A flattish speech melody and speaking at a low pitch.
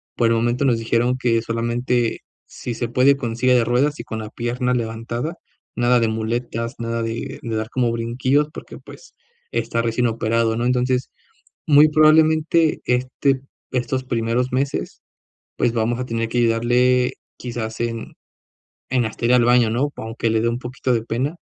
Yes: narrow, 1.7 semitones; low, 120 Hz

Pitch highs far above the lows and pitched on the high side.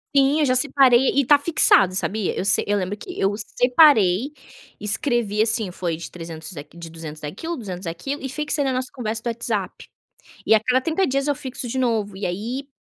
Yes: wide, 6.1 semitones; high, 230 Hz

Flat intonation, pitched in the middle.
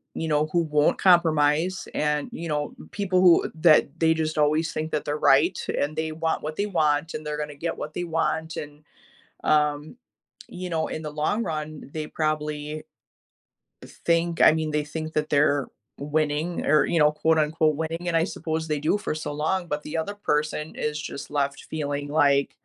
Yes: narrow, 1.5 semitones; medium, 155 Hz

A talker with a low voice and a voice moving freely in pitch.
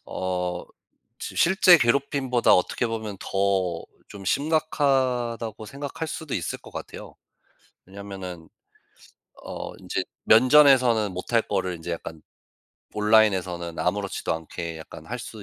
Yes: low, 105 Hz; wide, 6.0 semitones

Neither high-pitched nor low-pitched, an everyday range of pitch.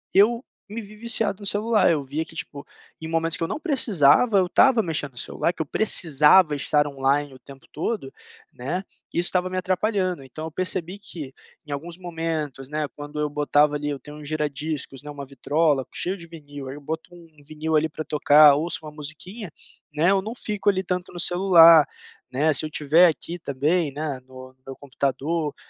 Yes: medium, 155 Hz; average, 3.9 semitones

